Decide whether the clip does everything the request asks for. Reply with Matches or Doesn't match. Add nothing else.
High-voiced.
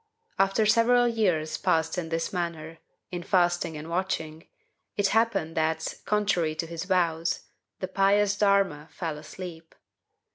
Doesn't match